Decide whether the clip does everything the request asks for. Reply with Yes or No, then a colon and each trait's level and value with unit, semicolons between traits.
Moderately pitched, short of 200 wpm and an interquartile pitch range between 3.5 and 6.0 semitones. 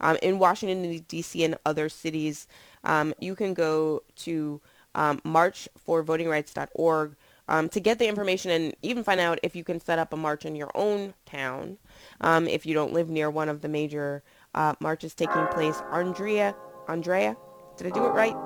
No: medium, 160 Hz; average, 180 wpm; narrow, 2.4 semitones